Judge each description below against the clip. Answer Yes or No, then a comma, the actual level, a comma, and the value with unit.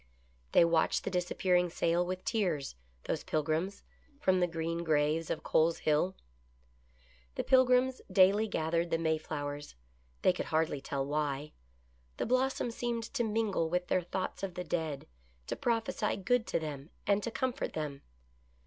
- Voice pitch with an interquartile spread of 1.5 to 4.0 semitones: No, average, 5.0 semitones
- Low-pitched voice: No, medium, 175 Hz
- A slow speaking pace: No, average, 165 wpm